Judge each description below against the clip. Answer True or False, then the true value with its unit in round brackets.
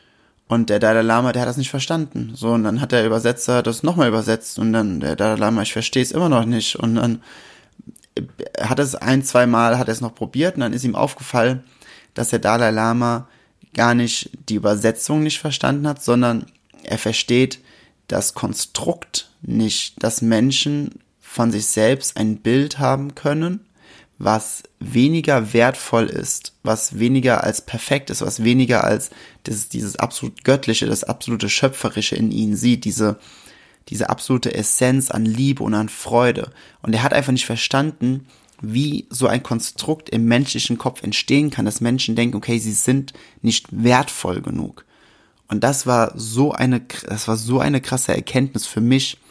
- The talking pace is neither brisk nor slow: True (170 wpm)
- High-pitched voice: False (120 Hz)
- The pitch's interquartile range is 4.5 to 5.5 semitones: False (2.8 semitones)